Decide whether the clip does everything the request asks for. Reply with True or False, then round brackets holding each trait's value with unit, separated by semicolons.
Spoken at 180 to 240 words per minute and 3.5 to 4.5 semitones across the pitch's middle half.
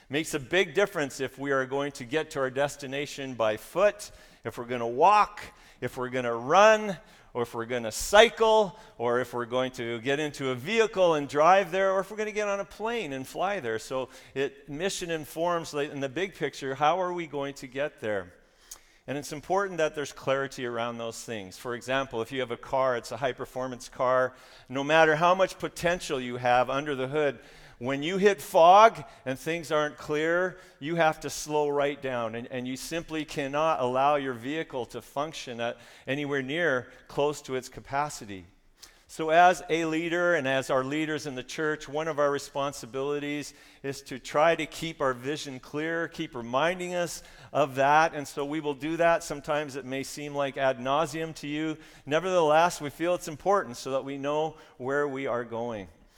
True (200 wpm; 3.8 semitones)